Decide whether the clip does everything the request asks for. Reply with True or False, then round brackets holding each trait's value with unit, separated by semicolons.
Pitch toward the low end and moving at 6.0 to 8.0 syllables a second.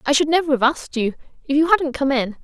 False (285 Hz; 6.5 syllables/s)